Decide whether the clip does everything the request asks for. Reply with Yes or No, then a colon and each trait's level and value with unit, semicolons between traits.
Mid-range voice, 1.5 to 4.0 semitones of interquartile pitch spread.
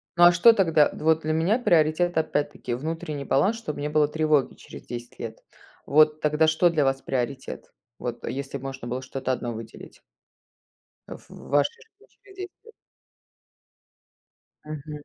Yes: medium, 150 Hz; average, 3.4 semitones